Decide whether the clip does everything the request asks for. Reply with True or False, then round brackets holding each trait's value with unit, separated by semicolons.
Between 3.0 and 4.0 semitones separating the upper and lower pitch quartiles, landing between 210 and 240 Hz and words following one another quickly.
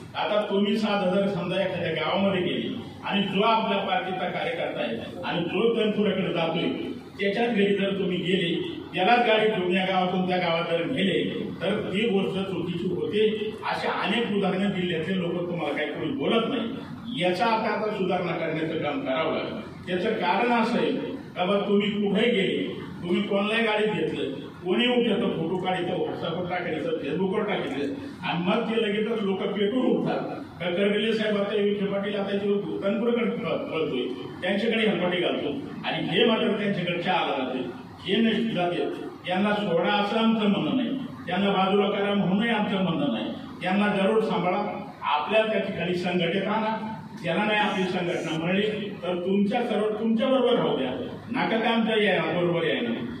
False (3.3 semitones; 200 Hz; 160 wpm)